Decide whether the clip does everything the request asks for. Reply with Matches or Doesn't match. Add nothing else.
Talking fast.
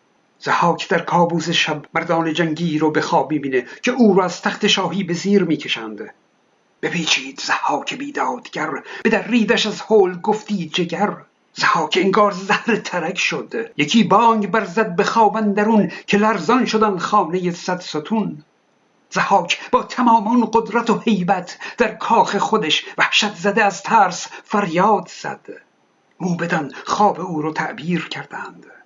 Doesn't match